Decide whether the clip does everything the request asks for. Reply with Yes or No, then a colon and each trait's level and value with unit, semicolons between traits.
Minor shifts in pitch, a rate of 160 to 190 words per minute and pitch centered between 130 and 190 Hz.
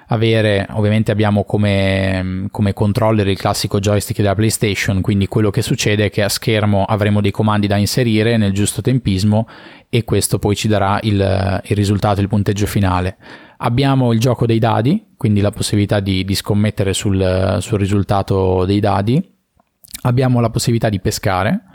No: narrow, 2.3 semitones; average, 165 wpm; low, 105 Hz